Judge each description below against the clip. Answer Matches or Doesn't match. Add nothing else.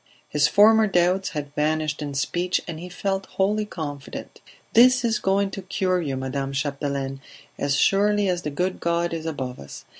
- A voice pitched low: Doesn't match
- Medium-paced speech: Matches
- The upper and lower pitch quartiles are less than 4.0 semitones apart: Doesn't match